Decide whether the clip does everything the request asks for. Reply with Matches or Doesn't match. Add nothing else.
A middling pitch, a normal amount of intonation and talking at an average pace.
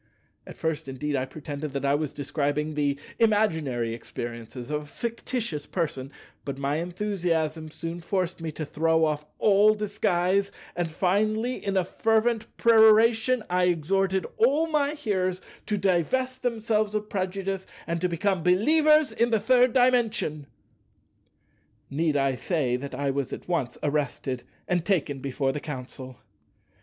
Doesn't match